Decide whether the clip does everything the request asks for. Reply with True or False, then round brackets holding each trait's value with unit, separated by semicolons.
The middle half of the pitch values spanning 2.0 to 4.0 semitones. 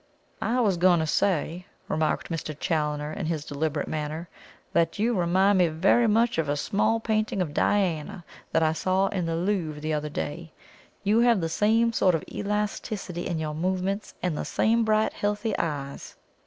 False (4.7 semitones)